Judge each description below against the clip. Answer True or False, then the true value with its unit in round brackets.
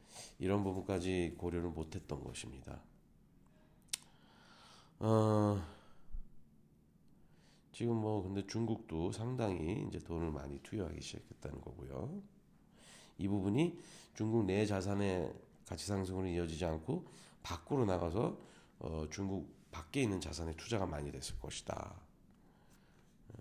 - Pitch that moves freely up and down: False (4.7 semitones)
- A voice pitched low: True (95 Hz)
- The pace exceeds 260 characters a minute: False (240 characters per minute)